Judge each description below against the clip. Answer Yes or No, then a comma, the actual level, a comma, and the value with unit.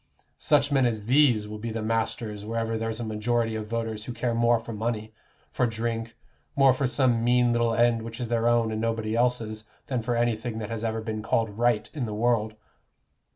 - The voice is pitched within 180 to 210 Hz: No, low, 115 Hz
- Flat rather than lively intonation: Yes, narrow, 1.5 semitones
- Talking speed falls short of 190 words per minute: No, fast, 205 wpm